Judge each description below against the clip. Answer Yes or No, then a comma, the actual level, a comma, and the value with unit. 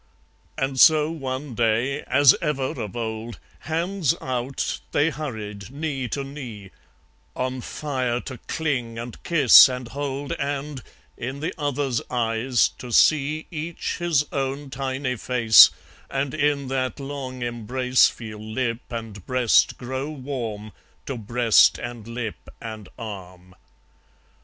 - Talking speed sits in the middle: No, slow, 130 wpm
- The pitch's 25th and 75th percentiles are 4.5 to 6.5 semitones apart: No, average, 3.4 semitones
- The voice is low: Yes, low, 130 Hz